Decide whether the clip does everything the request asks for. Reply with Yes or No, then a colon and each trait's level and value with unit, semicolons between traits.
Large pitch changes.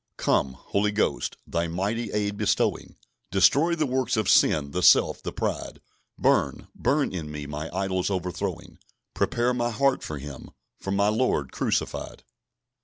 Yes: wide, 6.3 semitones